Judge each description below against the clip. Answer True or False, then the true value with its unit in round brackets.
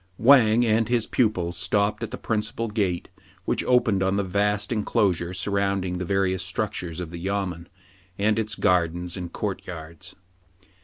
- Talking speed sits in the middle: True (160 wpm)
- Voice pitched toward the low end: True (100 Hz)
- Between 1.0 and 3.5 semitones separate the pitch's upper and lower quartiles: True (3.1 semitones)